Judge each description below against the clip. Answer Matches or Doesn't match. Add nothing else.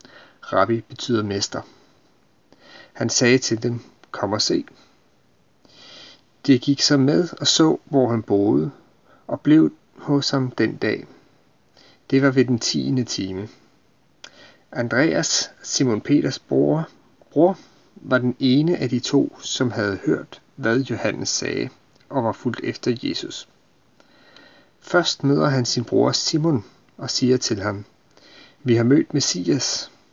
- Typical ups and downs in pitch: Matches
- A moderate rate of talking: Doesn't match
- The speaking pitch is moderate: Doesn't match